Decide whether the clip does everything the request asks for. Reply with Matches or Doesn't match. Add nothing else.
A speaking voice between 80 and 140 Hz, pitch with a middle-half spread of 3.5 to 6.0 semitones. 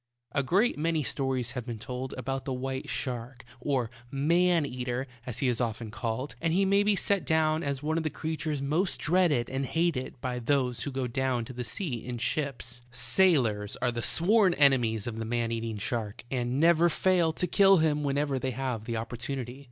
Matches